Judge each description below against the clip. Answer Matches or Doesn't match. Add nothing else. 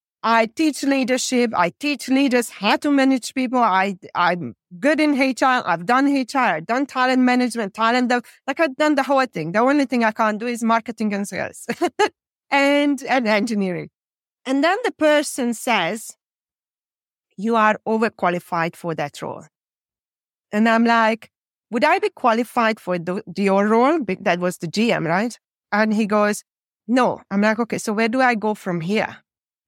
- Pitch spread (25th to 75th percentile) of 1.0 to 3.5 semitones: Doesn't match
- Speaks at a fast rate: Doesn't match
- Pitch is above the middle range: Matches